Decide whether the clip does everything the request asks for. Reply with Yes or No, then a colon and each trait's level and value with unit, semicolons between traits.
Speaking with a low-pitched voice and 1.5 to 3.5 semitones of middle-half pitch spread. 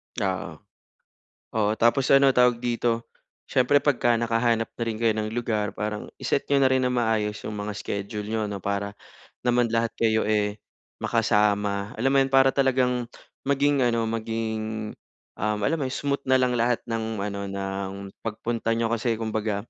Yes: low, 115 Hz; average, 2.7 semitones